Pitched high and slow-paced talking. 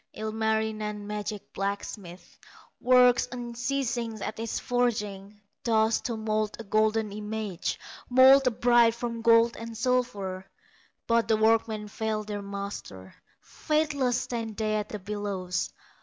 Yes: high, 220 Hz; slow, 125 wpm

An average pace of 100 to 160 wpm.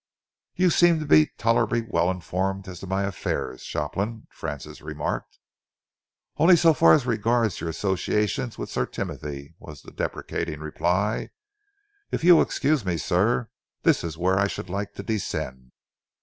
Yes: average, 155 wpm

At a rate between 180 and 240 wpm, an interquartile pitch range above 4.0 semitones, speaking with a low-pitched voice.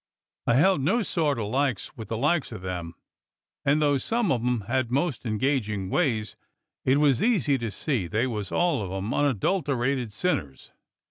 Yes: average, 185 wpm; average, 5.2 semitones; low, 130 Hz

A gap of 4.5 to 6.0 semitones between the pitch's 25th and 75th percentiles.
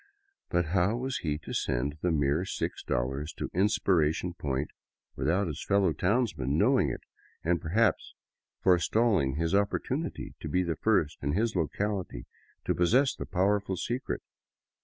Yes: average, 5.2 semitones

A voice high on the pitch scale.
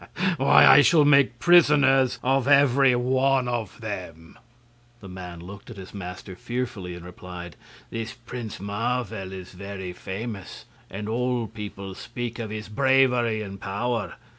No: low, 110 Hz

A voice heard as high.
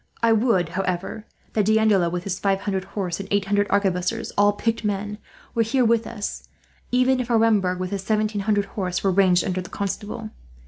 Yes: high, 205 Hz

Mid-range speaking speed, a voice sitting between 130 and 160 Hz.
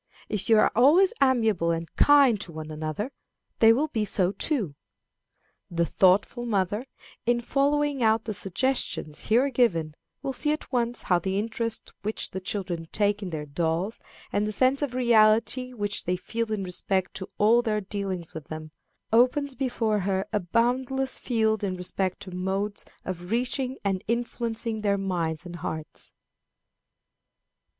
No: average, 160 wpm; high, 210 Hz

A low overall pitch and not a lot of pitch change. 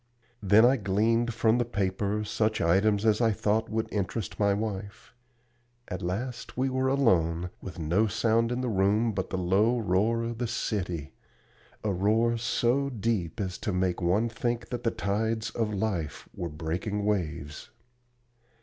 No: low, 105 Hz; average, 3.5 semitones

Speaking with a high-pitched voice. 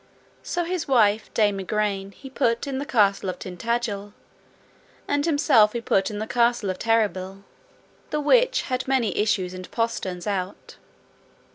Yes: high, 220 Hz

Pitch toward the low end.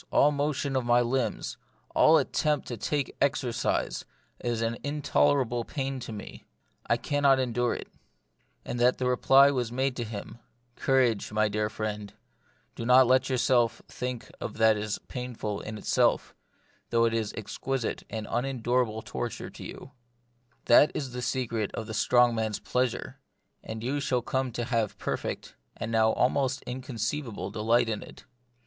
Yes: low, 120 Hz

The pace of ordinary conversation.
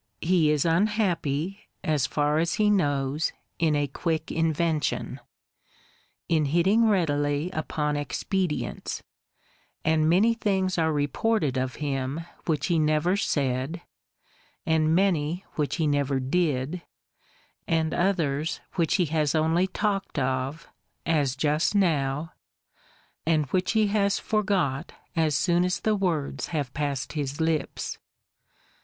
No: slow, 125 wpm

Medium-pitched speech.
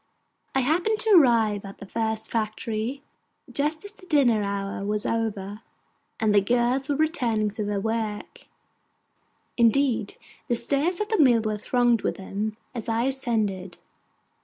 No: high, 230 Hz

